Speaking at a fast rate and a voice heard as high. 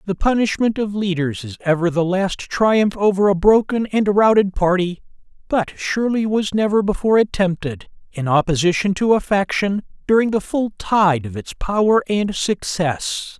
No: average, 155 wpm; high, 195 Hz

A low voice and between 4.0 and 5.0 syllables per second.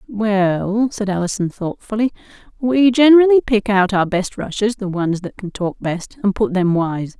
No: high, 205 Hz; 4.5 syllables/s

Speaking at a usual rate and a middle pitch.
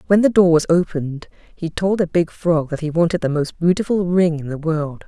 No: fast, 235 wpm; medium, 170 Hz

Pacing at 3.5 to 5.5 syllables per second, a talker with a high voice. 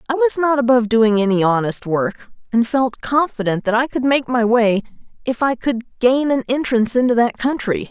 Yes: 5.3 syllables/s; high, 240 Hz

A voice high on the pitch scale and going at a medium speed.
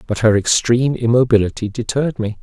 No: low, 115 Hz; average, 150 wpm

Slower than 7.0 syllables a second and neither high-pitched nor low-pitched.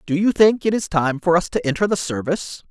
Yes: 6.0 syllables/s; medium, 175 Hz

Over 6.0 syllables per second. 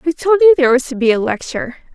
Yes: 7.1 syllables/s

